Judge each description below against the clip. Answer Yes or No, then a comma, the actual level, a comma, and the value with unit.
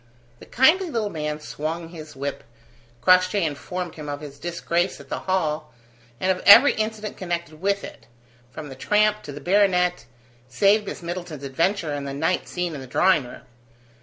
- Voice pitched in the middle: Yes, medium, 175 Hz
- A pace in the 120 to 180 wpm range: Yes, average, 175 wpm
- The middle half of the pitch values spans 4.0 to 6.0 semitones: Yes, average, 4.6 semitones